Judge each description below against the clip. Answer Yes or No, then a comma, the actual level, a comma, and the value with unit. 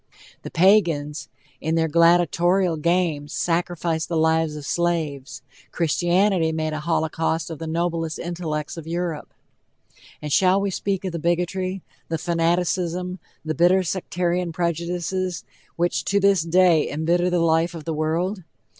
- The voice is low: No, medium, 170 Hz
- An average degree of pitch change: No, narrow, 1.9 semitones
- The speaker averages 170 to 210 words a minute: No, average, 140 wpm